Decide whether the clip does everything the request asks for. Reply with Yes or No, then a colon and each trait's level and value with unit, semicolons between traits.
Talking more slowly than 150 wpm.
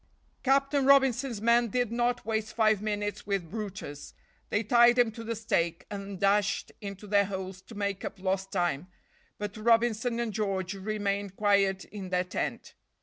No: average, 160 wpm